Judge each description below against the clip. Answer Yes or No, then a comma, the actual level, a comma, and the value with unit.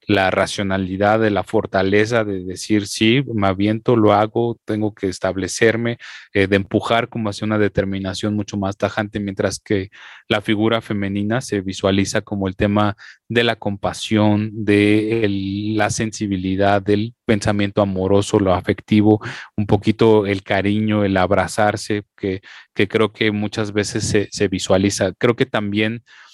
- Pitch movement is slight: Yes, narrow, 1.6 semitones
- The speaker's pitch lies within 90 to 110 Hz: Yes, low, 105 Hz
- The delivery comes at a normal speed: Yes, average, 150 wpm